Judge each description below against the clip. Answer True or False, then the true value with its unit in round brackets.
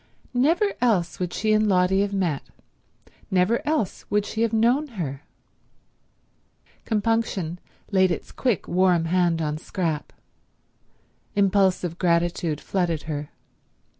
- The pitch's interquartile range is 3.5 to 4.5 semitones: True (4.0 semitones)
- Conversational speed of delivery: False (115 wpm)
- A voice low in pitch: False (185 Hz)